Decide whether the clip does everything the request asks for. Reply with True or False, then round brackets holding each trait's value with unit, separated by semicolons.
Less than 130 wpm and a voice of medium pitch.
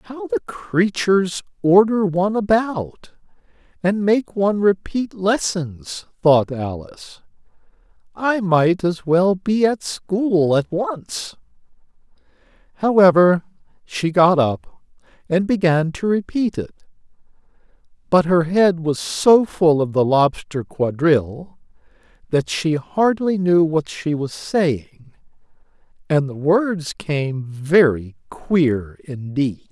True (115 wpm; 170 Hz)